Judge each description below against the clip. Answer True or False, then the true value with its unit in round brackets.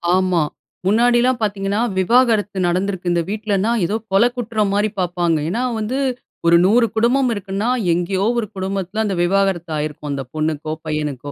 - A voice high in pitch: True (195 Hz)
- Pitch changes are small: False (4.0 semitones)